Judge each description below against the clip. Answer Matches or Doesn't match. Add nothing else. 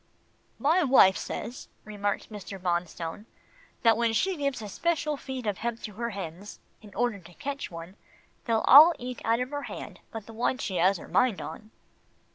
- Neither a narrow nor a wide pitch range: Matches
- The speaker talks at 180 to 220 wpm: Matches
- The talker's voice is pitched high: Matches